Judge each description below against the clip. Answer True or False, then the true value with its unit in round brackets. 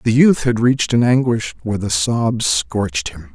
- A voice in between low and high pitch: False (110 Hz)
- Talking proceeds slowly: False (200 wpm)